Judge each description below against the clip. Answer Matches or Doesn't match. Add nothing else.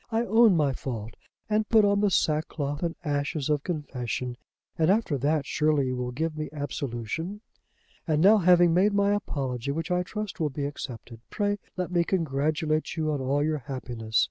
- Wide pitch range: Doesn't match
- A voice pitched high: Doesn't match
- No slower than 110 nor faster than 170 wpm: Doesn't match